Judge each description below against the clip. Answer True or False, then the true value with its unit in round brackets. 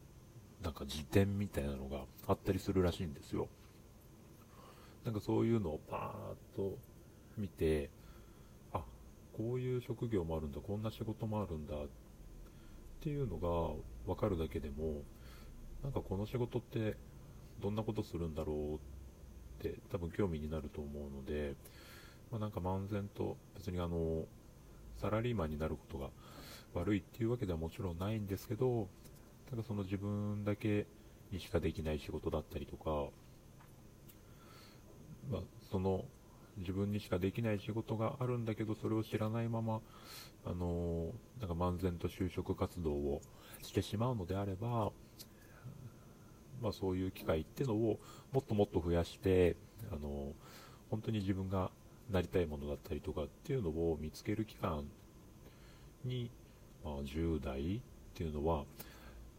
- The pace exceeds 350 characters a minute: False (275 characters per minute)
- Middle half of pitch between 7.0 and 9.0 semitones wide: False (5.6 semitones)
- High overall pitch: False (100 Hz)